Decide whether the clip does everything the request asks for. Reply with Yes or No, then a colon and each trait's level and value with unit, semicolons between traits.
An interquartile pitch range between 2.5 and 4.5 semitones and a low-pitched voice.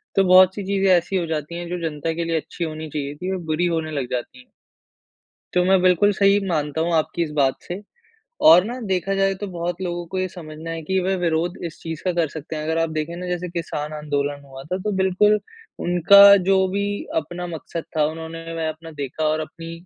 No: average, 2.8 semitones; medium, 170 Hz